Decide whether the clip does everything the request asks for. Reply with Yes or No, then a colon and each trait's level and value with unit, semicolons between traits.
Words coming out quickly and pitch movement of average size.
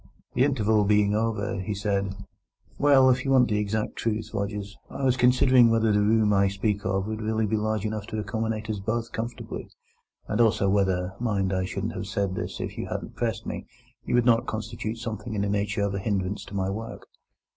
No: fast, 210 wpm; narrow, 2.1 semitones